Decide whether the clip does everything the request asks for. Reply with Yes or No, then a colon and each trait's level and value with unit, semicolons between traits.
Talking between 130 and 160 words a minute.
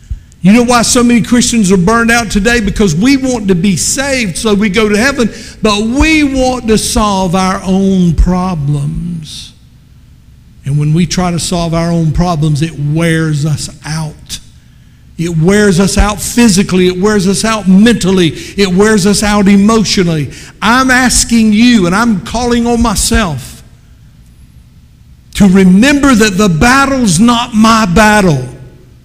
Yes: average, 150 wpm